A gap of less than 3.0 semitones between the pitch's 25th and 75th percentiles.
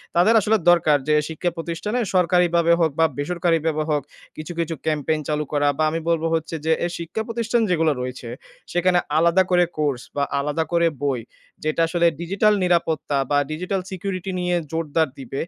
Yes: narrow, 2.6 semitones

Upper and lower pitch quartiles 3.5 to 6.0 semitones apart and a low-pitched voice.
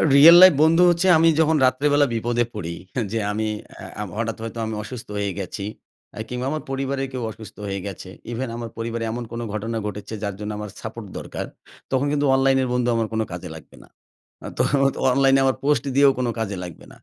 Yes: average, 4.1 semitones; low, 120 Hz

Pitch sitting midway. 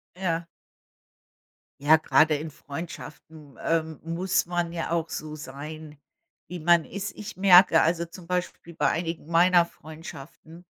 Yes: medium, 165 Hz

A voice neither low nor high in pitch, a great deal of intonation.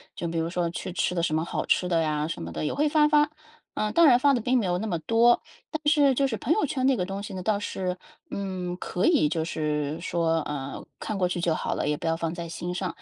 Yes: medium, 180 Hz; wide, 6.2 semitones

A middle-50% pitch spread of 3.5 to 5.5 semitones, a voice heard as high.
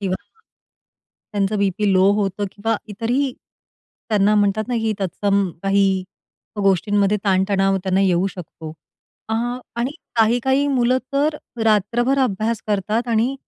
No: average, 3.0 semitones; high, 205 Hz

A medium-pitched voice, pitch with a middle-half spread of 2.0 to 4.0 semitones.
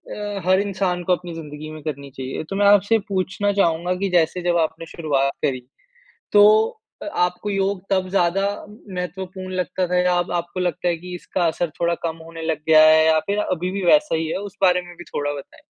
Yes: medium, 180 Hz; average, 2.8 semitones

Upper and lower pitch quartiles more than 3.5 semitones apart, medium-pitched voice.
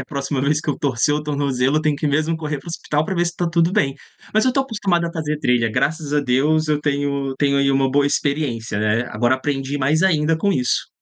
No: average, 2.9 semitones; medium, 145 Hz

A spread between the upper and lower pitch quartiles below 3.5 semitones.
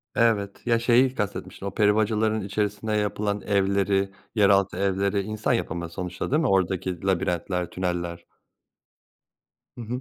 Yes: narrow, 2.4 semitones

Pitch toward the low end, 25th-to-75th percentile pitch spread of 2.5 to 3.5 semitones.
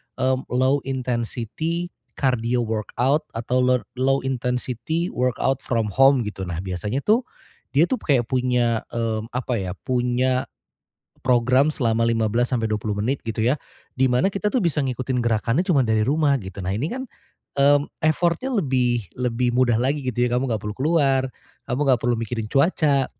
Yes: low, 125 Hz; average, 3.0 semitones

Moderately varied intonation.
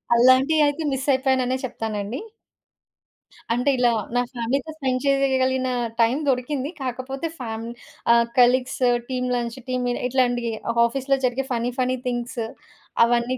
No: narrow, 1.6 semitones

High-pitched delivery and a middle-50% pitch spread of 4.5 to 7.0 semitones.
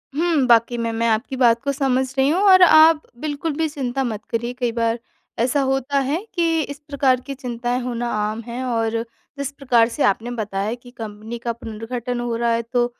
No: high, 245 Hz; average, 3.3 semitones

